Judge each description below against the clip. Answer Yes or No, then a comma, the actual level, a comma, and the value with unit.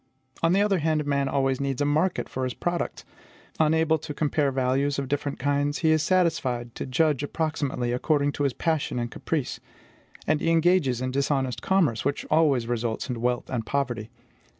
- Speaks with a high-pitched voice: No, medium, 140 Hz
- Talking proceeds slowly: No, average, 180 wpm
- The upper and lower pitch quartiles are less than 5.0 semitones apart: Yes, average, 3.6 semitones